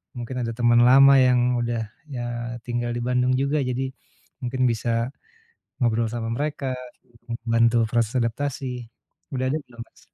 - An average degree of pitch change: No, narrow, 1.6 semitones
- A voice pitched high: No, low, 120 Hz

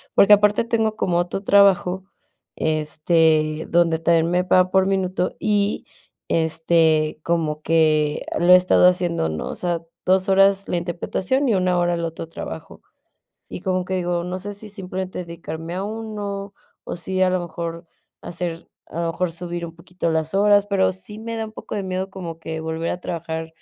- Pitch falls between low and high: Yes, medium, 180 Hz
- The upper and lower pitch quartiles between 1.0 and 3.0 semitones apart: Yes, average, 2.7 semitones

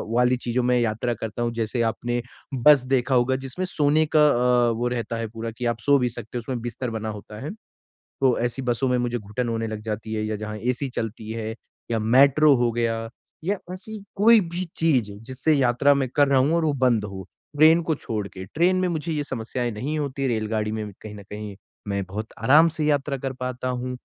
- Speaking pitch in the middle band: No, low, 125 Hz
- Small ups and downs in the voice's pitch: No, average, 3.8 semitones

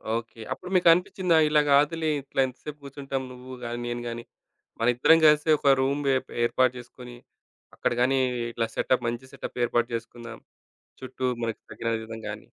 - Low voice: Yes, low, 130 Hz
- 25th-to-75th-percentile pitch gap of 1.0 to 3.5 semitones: Yes, average, 3.2 semitones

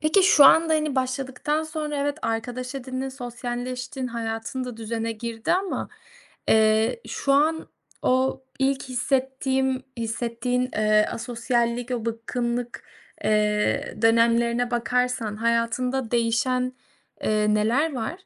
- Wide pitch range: No, narrow, 2.5 semitones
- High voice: Yes, high, 245 Hz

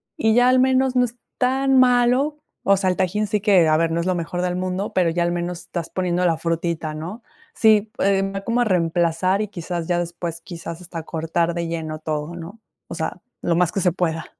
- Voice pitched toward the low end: No, medium, 180 Hz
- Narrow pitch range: No, average, 4.0 semitones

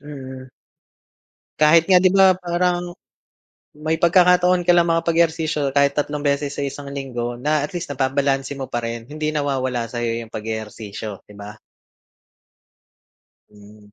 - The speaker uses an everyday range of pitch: No, wide, 5.7 semitones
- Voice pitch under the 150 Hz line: Yes, medium, 140 Hz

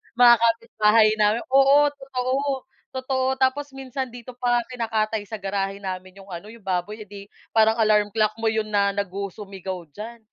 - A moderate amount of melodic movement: Yes, average, 3.9 semitones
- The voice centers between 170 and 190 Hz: No, high, 220 Hz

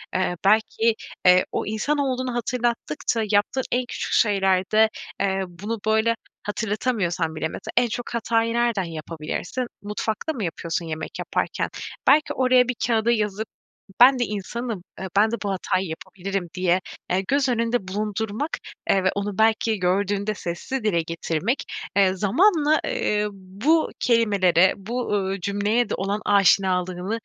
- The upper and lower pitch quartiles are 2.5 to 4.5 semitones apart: Yes, average, 3.9 semitones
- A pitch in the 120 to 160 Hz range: No, high, 210 Hz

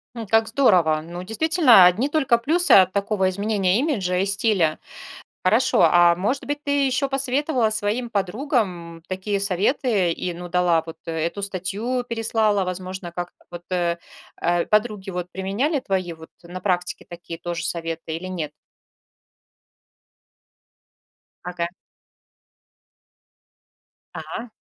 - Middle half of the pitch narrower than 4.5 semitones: No, average, 4.8 semitones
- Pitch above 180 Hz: Yes, high, 190 Hz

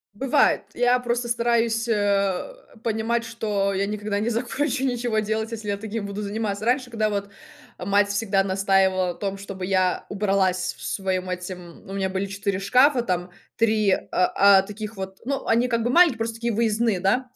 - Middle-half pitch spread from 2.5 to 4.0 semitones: Yes, average, 3.1 semitones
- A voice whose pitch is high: Yes, high, 210 Hz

